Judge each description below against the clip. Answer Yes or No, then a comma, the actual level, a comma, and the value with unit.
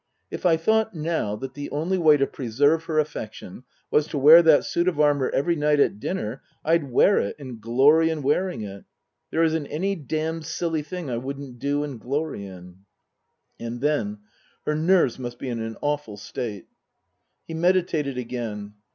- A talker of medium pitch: Yes, medium, 145 Hz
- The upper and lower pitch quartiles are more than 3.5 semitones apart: Yes, average, 5.0 semitones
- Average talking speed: Yes, average, 180 wpm